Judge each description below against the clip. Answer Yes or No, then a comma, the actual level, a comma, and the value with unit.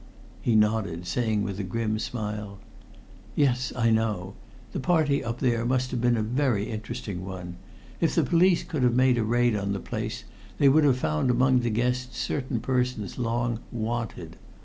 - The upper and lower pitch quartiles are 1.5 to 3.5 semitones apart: Yes, average, 2.9 semitones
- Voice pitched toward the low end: Yes, low, 120 Hz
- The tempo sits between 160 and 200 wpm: Yes, average, 175 wpm